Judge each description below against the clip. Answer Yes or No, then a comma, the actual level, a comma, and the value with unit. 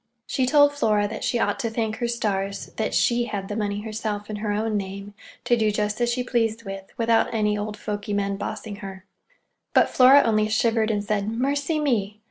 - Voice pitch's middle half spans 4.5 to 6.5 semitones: No, narrow, 2.4 semitones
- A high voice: Yes, high, 215 Hz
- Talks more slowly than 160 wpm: No, fast, 205 wpm